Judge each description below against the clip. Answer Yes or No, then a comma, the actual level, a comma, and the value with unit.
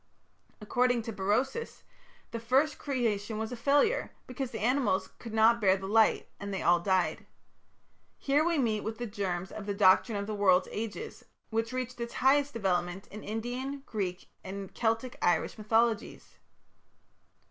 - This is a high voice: Yes, high, 225 Hz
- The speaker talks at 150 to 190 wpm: Yes, average, 160 wpm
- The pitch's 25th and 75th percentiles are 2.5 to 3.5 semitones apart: No, average, 3.9 semitones